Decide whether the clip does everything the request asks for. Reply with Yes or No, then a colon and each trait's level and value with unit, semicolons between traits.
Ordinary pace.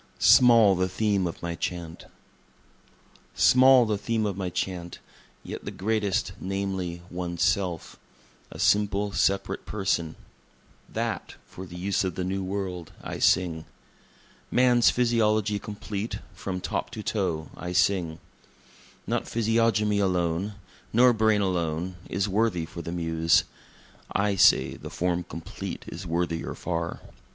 No: slow, 130 wpm